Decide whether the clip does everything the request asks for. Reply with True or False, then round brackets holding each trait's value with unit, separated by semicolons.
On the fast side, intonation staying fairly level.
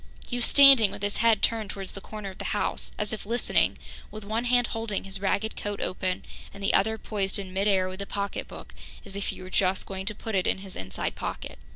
True (240 wpm; 2.3 semitones)